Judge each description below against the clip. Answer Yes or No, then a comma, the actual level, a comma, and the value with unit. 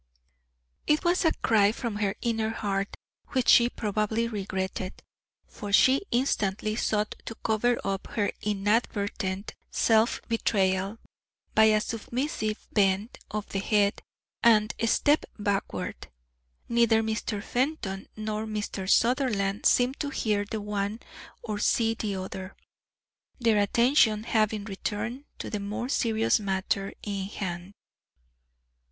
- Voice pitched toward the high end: Yes, high, 215 Hz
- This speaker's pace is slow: Yes, slow, 125 wpm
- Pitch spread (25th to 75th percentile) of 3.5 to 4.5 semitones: No, narrow, 2.4 semitones